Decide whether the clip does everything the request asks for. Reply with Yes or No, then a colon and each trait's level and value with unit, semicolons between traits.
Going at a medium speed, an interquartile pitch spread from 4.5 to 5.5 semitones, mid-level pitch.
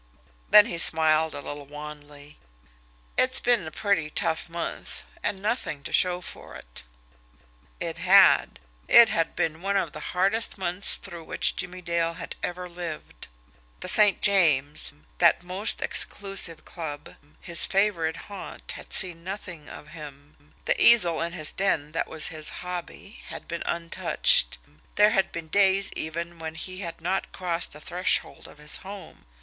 No: average, 155 wpm; average, 3.5 semitones; medium, 170 Hz